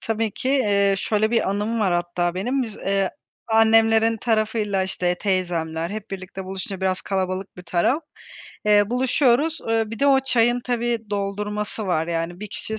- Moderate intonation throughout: Yes, average, 3.3 semitones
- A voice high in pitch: Yes, high, 210 Hz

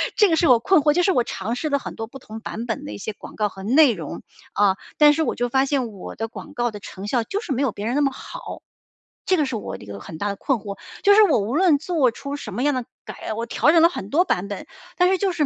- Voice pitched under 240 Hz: No, very high, 255 Hz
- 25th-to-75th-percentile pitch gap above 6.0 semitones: Yes, wide, 6.4 semitones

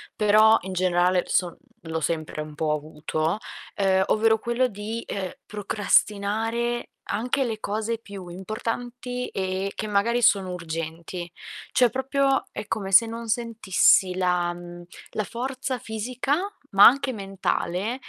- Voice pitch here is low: No, high, 205 Hz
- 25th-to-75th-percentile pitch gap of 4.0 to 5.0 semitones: Yes, average, 4.3 semitones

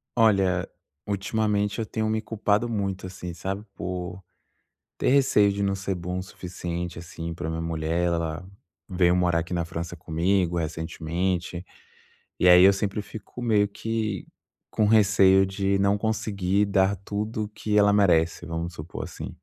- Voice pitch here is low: Yes, very low, 95 Hz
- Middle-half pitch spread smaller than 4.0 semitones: Yes, average, 3.0 semitones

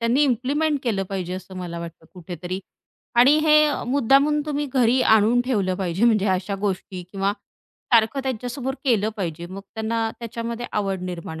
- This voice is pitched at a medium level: No, high, 220 Hz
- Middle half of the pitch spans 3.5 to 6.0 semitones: Yes, average, 5.1 semitones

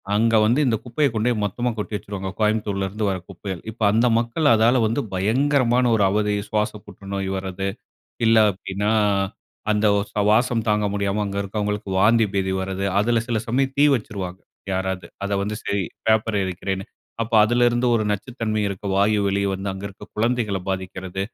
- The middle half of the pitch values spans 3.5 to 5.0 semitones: No, average, 2.9 semitones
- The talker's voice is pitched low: Yes, low, 105 Hz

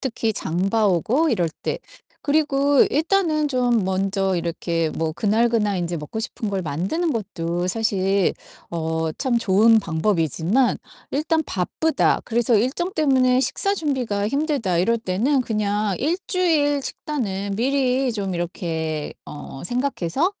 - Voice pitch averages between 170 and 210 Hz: No, high, 220 Hz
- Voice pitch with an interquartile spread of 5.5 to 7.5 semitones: Yes, wide, 7.1 semitones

